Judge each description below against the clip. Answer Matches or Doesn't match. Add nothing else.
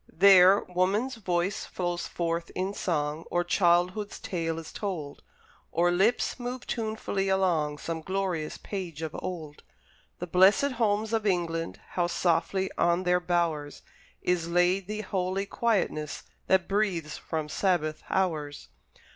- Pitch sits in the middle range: Matches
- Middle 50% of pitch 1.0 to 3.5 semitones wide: Matches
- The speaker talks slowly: Matches